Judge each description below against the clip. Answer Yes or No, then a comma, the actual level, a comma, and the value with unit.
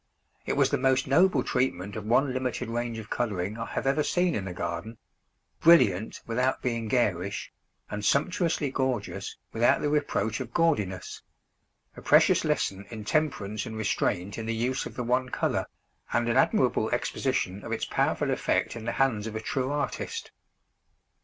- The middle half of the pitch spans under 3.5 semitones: No, average, 4.1 semitones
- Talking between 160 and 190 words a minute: Yes, average, 170 wpm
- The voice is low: Yes, low, 115 Hz